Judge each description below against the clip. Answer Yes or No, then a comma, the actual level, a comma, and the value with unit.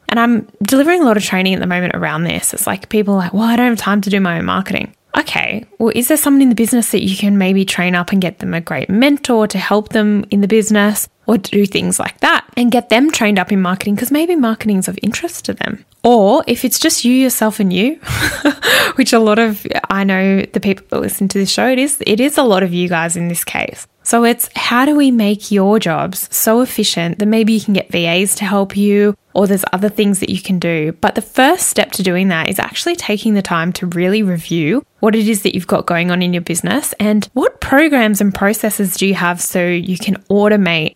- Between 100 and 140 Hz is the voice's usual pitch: No, high, 205 Hz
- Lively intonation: No, average, 3.6 semitones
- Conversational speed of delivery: No, fast, 250 wpm